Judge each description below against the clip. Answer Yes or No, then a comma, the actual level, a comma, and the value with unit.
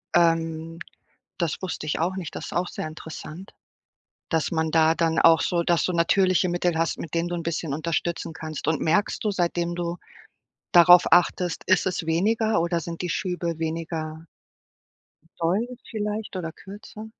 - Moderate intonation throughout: No, narrow, 1.9 semitones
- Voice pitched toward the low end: No, medium, 170 Hz